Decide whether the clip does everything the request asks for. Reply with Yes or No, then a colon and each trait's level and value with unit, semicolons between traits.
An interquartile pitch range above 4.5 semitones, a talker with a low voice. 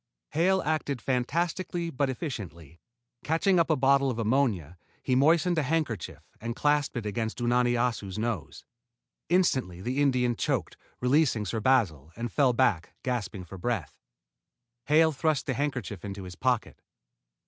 Yes: wide, 5.5 semitones; low, 125 Hz